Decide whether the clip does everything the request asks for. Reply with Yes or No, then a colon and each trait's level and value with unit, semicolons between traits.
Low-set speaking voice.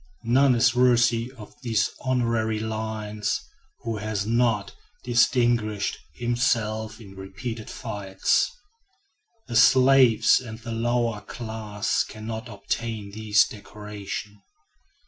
Yes: low, 110 Hz